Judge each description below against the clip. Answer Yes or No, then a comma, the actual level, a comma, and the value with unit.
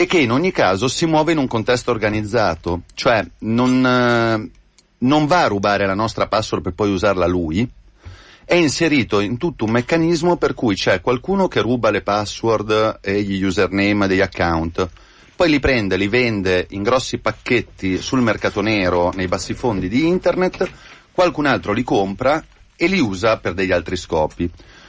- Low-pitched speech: Yes, low, 110 Hz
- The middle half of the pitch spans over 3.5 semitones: Yes, average, 5.0 semitones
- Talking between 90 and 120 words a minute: No, fast, 170 wpm